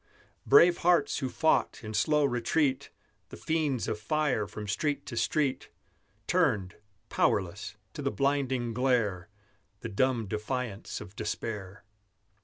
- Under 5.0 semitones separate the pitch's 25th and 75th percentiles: No, average, 5.3 semitones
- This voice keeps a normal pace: No, slow, 125 wpm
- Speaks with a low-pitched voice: Yes, low, 125 Hz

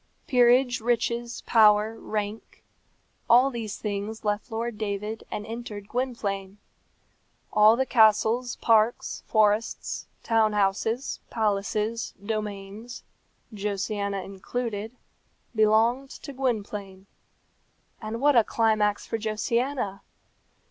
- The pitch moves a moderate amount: No, narrow, 2.3 semitones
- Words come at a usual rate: No, slow, 95 wpm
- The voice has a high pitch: Yes, high, 220 Hz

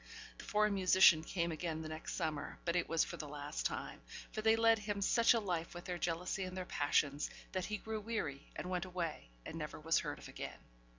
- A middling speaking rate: No, fast, 225 wpm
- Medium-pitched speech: Yes, medium, 175 Hz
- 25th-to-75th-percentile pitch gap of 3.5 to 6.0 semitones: Yes, average, 4.2 semitones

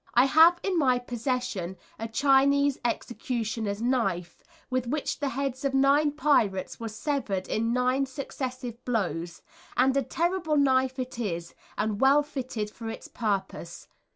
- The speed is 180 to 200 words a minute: No, average, 145 wpm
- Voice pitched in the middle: No, very high, 255 Hz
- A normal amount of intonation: Yes, average, 3.9 semitones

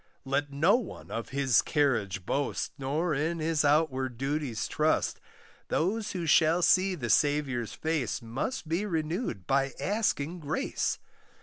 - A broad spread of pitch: No, average, 3.9 semitones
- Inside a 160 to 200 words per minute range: No, slow, 135 wpm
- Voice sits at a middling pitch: Yes, medium, 150 Hz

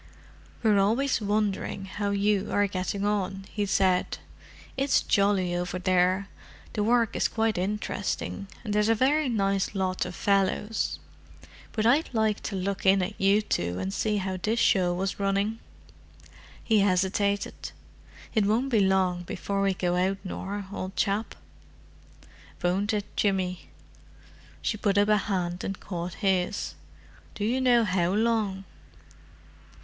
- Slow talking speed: No, average, 145 wpm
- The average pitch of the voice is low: No, high, 200 Hz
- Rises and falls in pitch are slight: Yes, narrow, 2.2 semitones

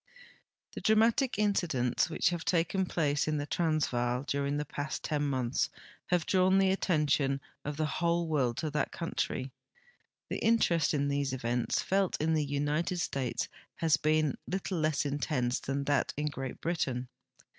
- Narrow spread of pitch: No, average, 3.5 semitones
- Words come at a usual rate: Yes, average, 160 wpm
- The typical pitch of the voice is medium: Yes, medium, 150 Hz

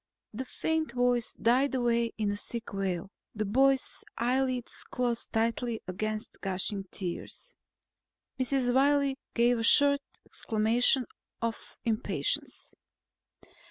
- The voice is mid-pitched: No, high, 235 Hz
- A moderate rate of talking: No, slow, 110 wpm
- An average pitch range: Yes, average, 3.3 semitones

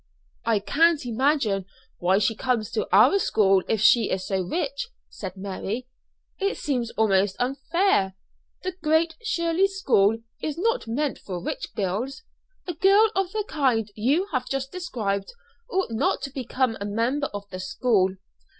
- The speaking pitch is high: Yes, very high, 250 Hz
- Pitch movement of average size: No, wide, 8.2 semitones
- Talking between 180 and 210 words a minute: No, average, 155 wpm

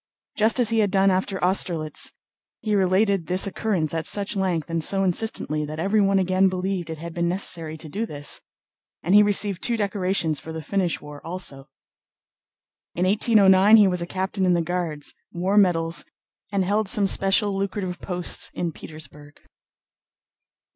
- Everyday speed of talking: Yes, average, 165 wpm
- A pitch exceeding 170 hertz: Yes, medium, 185 Hz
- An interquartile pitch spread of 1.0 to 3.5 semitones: Yes, average, 3.2 semitones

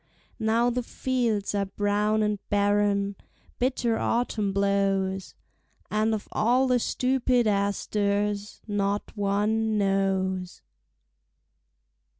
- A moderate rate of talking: No, slow, 95 wpm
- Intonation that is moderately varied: No, narrow, 2.0 semitones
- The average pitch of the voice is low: No, high, 205 Hz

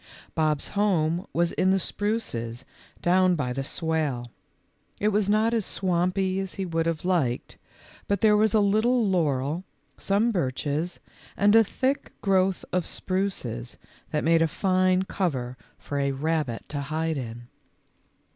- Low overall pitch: No, medium, 175 Hz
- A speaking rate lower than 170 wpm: Yes, average, 145 wpm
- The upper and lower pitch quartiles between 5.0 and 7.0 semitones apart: Yes, average, 5.3 semitones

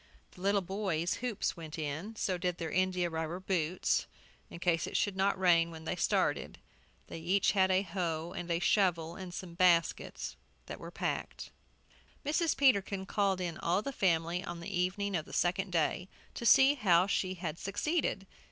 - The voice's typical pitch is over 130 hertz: Yes, medium, 185 Hz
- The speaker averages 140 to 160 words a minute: No, average, 175 wpm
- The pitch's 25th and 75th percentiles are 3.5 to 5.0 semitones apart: No, average, 2.7 semitones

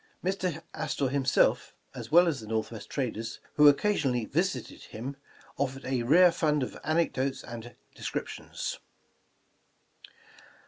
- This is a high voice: No, low, 135 Hz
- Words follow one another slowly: Yes, slow, 120 wpm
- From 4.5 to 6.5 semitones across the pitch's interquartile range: Yes, average, 5.0 semitones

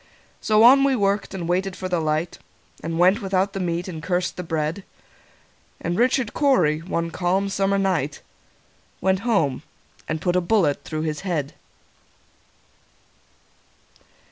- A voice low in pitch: No, medium, 180 Hz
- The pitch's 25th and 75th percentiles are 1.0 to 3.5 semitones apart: Yes, average, 3.2 semitones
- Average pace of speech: No, slow, 130 wpm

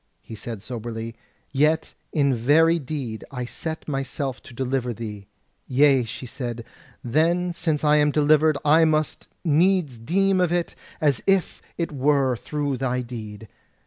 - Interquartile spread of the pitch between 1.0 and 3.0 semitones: No, average, 4.4 semitones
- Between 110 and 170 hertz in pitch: Yes, medium, 140 Hz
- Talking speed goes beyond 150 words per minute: No, average, 145 wpm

